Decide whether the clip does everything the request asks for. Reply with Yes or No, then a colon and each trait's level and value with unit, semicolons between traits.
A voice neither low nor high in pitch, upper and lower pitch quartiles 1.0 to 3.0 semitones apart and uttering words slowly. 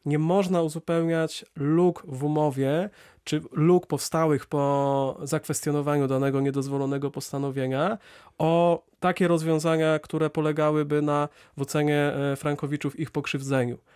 Yes: medium, 150 Hz; narrow, 2.5 semitones; slow, 105 wpm